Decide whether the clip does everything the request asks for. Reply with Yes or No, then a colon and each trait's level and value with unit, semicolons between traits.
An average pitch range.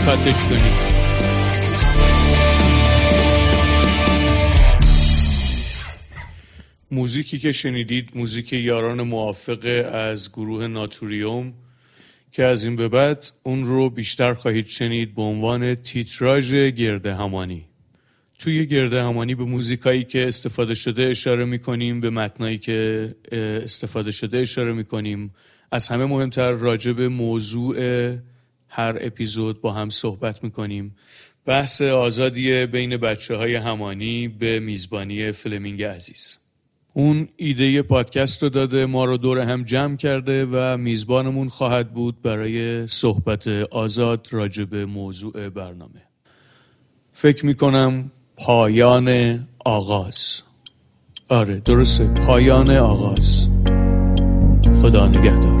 Yes: average, 3.4 semitones